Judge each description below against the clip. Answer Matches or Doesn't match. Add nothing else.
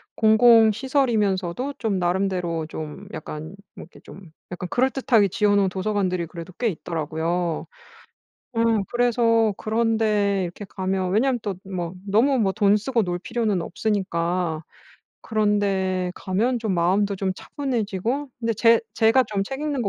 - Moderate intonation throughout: Matches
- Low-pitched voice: Doesn't match